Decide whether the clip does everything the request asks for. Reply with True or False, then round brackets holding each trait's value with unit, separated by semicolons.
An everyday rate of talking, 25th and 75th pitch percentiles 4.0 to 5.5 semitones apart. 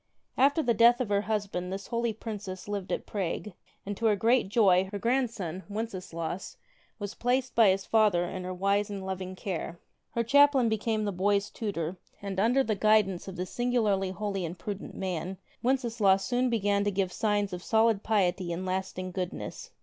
False (180 wpm; 3.2 semitones)